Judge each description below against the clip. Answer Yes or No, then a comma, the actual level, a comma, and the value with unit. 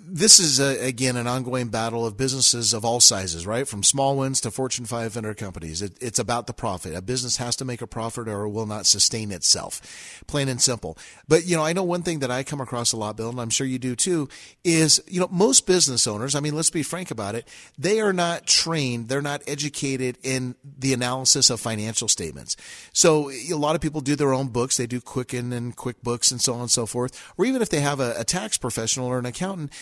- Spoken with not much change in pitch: No, average, 3.7 semitones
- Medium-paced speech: No, fast, 240 wpm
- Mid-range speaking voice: No, low, 125 Hz